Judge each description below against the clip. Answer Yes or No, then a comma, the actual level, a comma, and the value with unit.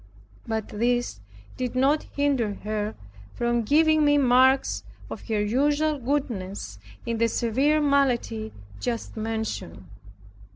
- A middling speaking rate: No, slow, 115 wpm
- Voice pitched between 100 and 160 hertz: No, high, 240 Hz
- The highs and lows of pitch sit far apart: No, average, 4.4 semitones